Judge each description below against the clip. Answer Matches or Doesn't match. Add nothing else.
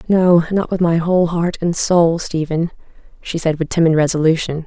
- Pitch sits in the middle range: Matches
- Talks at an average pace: Matches